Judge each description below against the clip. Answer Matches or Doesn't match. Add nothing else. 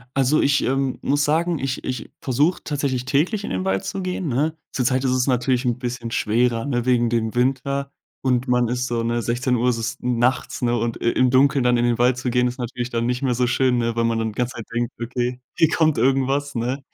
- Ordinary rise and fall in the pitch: Doesn't match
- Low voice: Matches